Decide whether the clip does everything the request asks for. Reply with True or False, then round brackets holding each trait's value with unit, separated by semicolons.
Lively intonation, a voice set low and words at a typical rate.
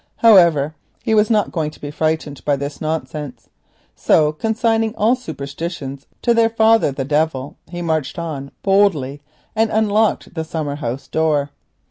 False (6.7 semitones; 160 Hz; 150 wpm)